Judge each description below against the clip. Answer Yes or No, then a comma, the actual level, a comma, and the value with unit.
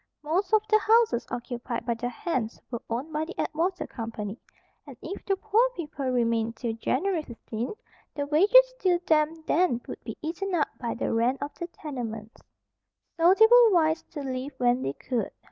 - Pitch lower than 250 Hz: No, very high, 295 Hz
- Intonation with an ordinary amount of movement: No, wide, 7.2 semitones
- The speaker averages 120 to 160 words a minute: No, average, 180 wpm